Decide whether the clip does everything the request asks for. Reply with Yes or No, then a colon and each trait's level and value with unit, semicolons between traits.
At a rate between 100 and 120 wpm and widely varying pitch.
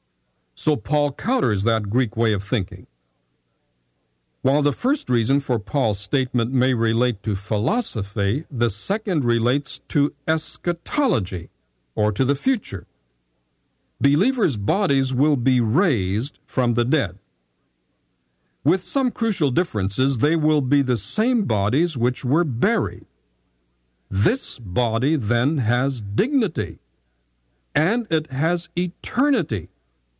Yes: slow, 115 wpm; wide, 8.2 semitones